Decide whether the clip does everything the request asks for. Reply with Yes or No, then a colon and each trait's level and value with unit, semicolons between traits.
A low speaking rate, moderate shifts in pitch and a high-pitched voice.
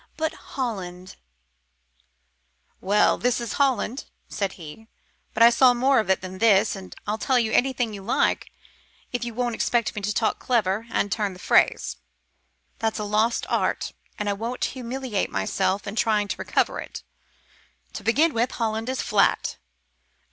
No: average, 165 wpm; average, 3.6 semitones; high, 220 Hz